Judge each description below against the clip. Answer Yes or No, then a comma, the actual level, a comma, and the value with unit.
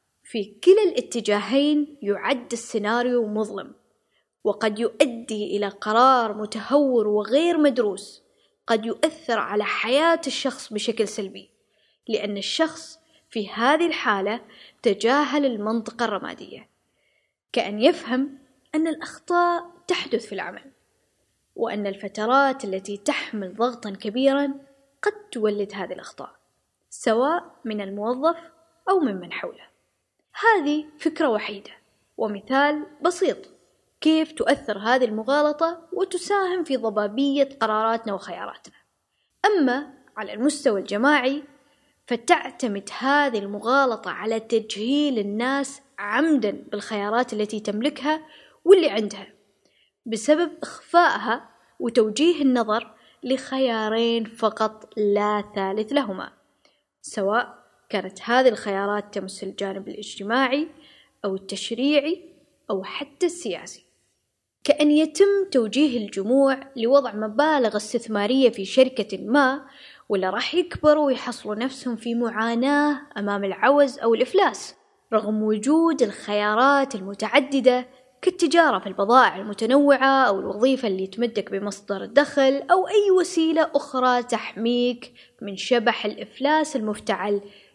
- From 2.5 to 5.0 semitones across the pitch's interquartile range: No, wide, 5.6 semitones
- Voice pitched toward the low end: No, very high, 250 Hz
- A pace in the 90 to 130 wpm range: Yes, average, 100 wpm